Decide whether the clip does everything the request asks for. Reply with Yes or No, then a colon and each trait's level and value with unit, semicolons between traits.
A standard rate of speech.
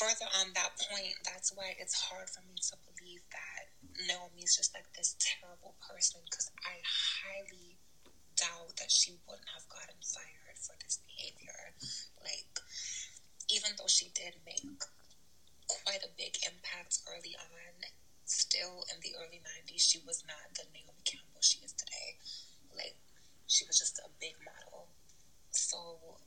Yes: average, 150 wpm